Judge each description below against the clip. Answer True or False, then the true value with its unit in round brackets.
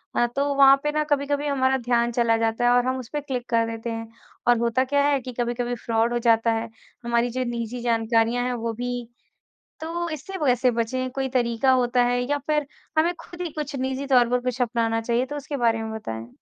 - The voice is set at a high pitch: True (245 Hz)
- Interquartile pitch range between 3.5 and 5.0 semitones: False (2.7 semitones)